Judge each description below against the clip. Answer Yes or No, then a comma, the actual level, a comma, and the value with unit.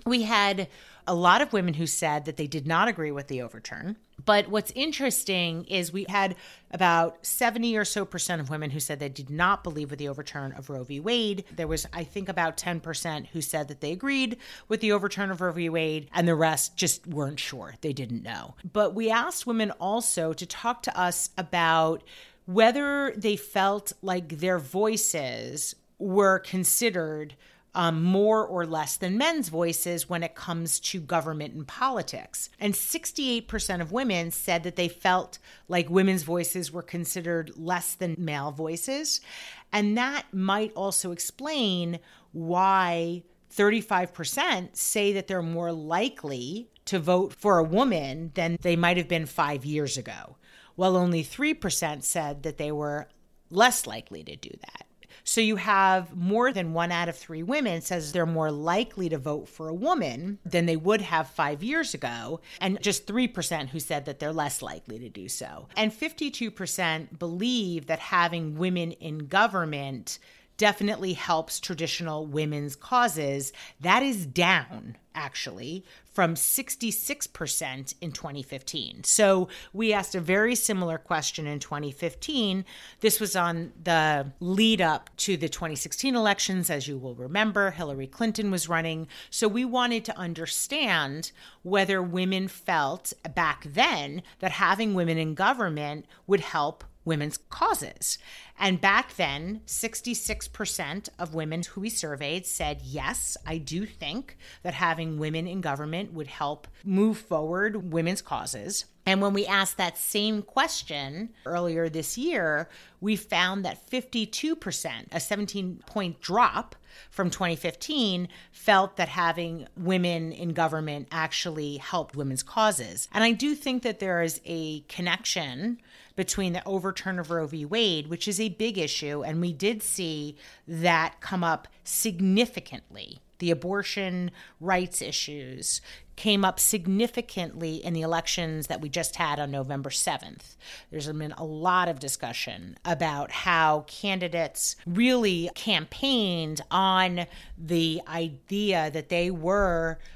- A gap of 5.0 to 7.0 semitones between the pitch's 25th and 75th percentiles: No, average, 4.1 semitones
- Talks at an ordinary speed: Yes, average, 150 wpm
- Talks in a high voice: No, medium, 175 Hz